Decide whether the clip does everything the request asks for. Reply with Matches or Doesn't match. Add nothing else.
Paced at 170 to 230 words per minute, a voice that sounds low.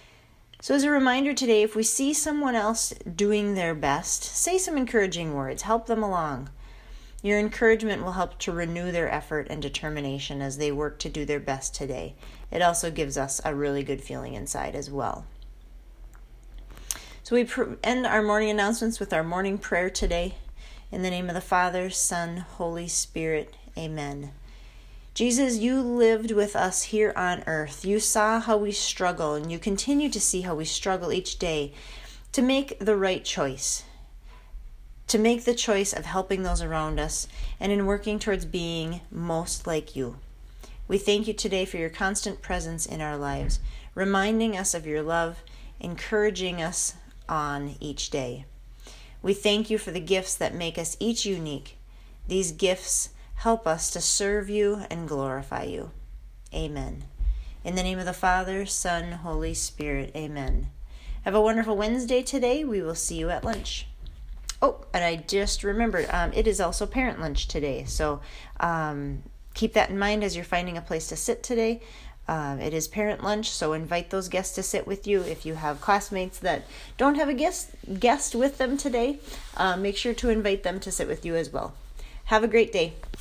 Doesn't match